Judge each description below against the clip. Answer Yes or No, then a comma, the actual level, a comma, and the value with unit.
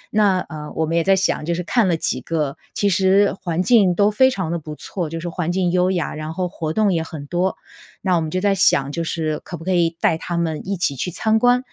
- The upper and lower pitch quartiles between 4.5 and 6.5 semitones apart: No, average, 2.9 semitones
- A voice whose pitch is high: No, medium, 175 Hz